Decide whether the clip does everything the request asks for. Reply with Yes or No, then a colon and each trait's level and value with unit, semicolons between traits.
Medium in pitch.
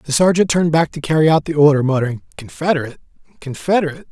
Yes: medium, 150 Hz